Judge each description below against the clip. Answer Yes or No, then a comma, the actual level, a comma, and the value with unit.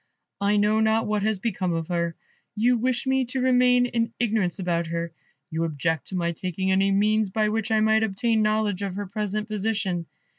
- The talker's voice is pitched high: Yes, high, 210 Hz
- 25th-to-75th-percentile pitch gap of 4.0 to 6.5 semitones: No, average, 3.4 semitones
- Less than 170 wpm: No, average, 195 wpm